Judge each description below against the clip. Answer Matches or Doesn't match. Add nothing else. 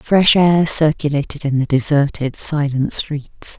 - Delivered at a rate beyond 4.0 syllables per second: Doesn't match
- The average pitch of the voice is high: Doesn't match